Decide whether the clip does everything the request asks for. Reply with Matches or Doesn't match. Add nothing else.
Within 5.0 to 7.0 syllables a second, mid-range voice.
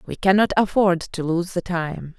Doesn't match